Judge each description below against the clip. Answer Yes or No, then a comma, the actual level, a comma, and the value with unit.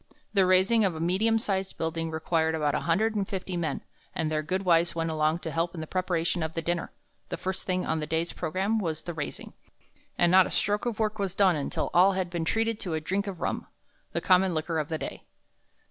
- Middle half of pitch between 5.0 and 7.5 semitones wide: No, average, 3.1 semitones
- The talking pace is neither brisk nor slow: No, fast, 235 wpm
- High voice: No, medium, 175 Hz